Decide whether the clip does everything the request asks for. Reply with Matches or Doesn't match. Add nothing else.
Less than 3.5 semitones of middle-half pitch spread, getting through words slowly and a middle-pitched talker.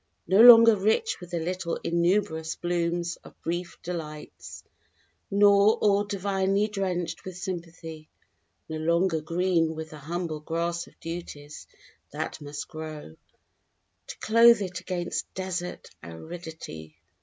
Matches